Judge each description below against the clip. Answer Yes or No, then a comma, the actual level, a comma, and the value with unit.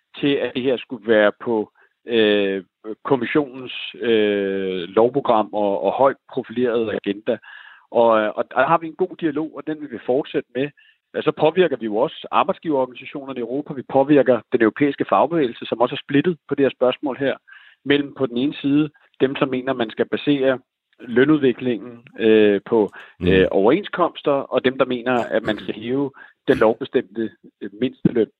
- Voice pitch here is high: No, low, 130 Hz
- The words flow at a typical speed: Yes, average, 170 wpm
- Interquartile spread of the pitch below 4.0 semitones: No, average, 4.4 semitones